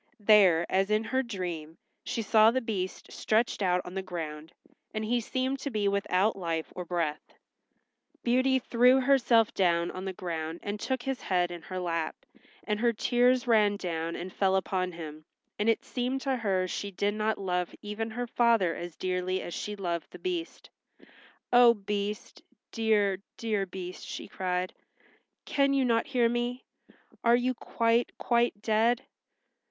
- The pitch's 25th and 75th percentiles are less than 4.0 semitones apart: No, average, 4.7 semitones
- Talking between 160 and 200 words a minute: Yes, average, 165 wpm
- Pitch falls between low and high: No, high, 210 Hz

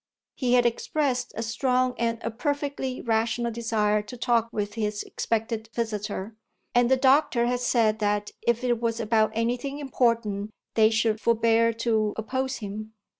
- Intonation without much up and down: Yes, narrow, 2.2 semitones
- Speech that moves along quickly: No, average, 155 wpm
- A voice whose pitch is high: Yes, high, 230 Hz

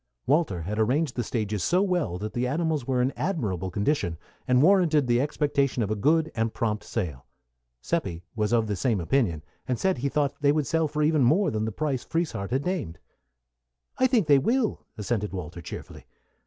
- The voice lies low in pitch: Yes, low, 125 Hz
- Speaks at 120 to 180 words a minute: No, average, 195 wpm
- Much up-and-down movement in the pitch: Yes, wide, 6.6 semitones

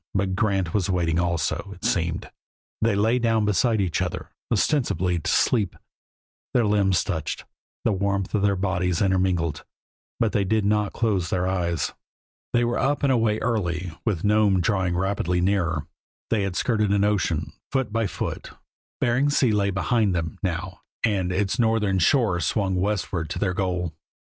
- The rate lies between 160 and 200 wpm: Yes, average, 165 wpm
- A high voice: No, low, 100 Hz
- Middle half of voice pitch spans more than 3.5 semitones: No, average, 3.2 semitones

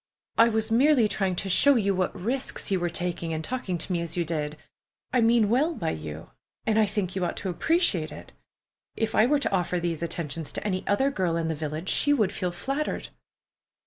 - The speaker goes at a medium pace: No, fast, 215 wpm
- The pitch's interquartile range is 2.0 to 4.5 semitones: No, average, 5.3 semitones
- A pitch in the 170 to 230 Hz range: Yes, high, 190 Hz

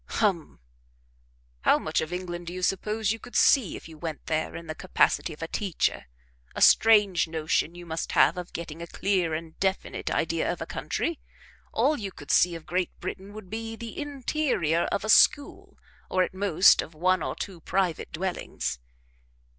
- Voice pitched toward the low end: No, medium, 180 Hz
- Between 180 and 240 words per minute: Yes, average, 185 wpm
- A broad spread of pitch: No, average, 4.0 semitones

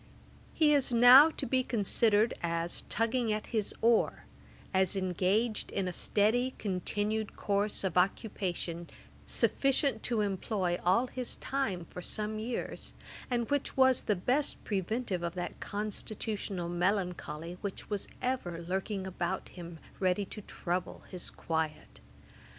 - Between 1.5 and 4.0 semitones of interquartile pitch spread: No, average, 4.4 semitones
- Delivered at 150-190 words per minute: No, average, 140 wpm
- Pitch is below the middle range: No, high, 205 Hz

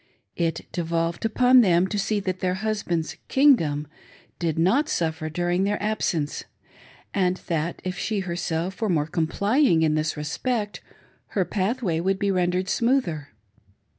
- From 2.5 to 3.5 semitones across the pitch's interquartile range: No, average, 4.2 semitones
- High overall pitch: No, medium, 180 Hz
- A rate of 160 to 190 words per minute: No, average, 140 wpm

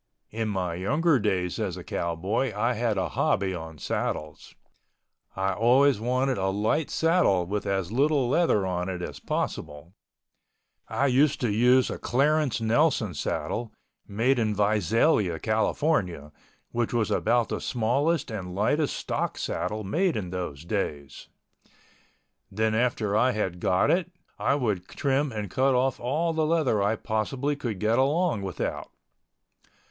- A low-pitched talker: Yes, low, 110 Hz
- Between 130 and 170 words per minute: Yes, average, 145 wpm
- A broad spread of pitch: Yes, wide, 5.9 semitones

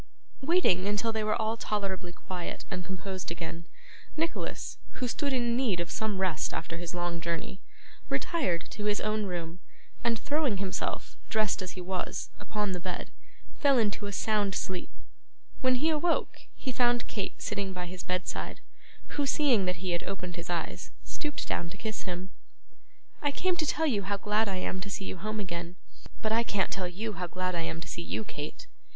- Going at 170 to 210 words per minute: Yes, average, 190 wpm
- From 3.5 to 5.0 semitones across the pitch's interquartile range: Yes, average, 4.1 semitones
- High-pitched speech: Yes, high, 195 Hz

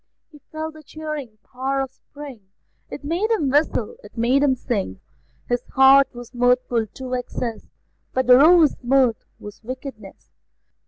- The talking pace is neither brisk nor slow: Yes, average, 150 wpm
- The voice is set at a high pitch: Yes, very high, 260 Hz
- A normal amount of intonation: Yes, average, 3.2 semitones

